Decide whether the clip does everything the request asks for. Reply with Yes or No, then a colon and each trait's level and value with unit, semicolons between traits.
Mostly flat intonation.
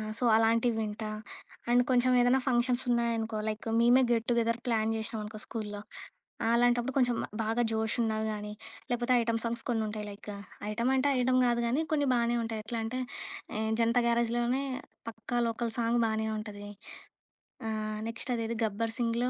Yes: narrow, 1.6 semitones